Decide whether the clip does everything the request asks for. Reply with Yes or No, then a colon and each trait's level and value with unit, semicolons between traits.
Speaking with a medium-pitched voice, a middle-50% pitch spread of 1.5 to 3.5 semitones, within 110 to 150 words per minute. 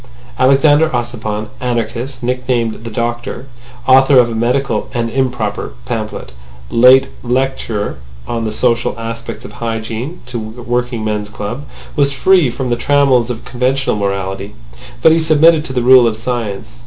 No: low, 120 Hz; average, 2.8 semitones; average, 140 wpm